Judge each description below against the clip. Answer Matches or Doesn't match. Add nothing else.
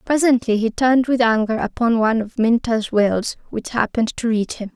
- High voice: Matches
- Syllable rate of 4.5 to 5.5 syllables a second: Matches